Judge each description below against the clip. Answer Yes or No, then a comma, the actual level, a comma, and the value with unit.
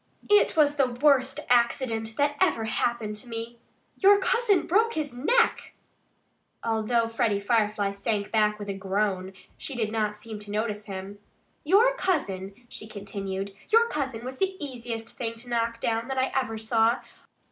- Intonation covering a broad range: No, average, 4.2 semitones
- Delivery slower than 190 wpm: Yes, average, 165 wpm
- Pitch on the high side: Yes, high, 230 Hz